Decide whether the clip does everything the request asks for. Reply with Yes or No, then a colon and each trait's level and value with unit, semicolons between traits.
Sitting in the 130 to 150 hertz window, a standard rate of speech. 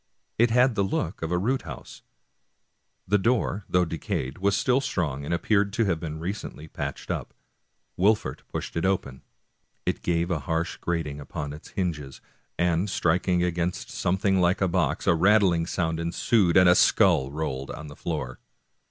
No: very low, 85 Hz; average, 170 wpm